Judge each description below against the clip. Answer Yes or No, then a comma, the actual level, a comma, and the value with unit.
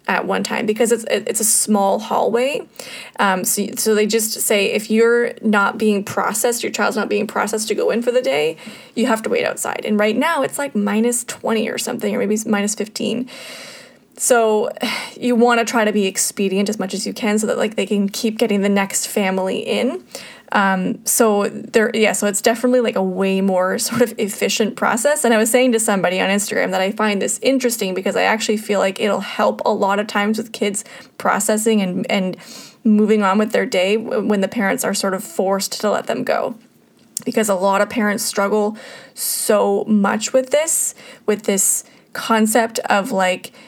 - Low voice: No, high, 215 Hz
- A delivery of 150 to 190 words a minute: No, fast, 205 wpm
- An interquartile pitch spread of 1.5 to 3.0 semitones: Yes, narrow, 2.6 semitones